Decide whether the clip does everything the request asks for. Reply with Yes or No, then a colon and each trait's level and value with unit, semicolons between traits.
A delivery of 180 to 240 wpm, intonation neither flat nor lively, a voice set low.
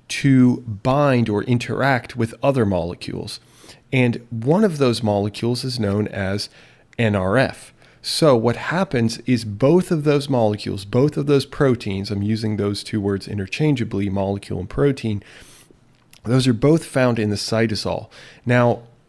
No: average, 140 wpm; average, 4.4 semitones; low, 120 Hz